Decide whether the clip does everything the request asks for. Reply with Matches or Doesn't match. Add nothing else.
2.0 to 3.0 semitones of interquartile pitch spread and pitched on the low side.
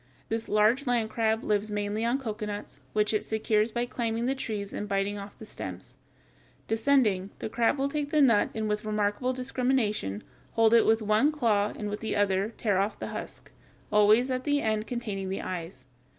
Doesn't match